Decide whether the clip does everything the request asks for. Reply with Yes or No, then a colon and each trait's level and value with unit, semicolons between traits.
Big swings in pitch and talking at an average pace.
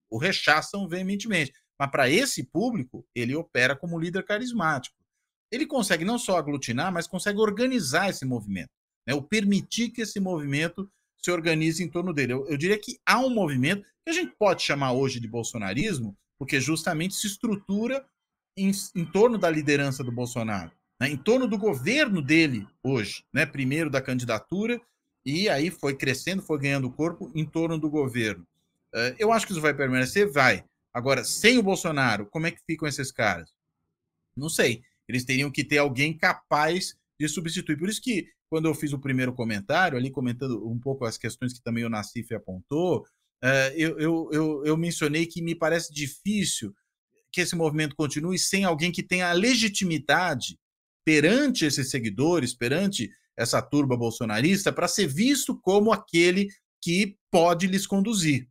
Yes: wide, 6.3 semitones; average, 170 wpm